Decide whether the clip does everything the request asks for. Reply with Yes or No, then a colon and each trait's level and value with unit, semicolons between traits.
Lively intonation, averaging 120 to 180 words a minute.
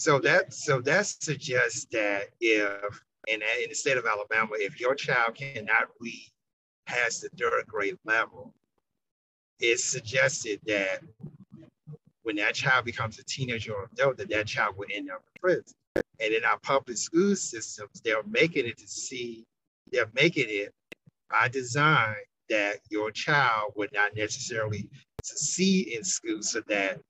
Yes: wide, 9.0 semitones; average, 155 wpm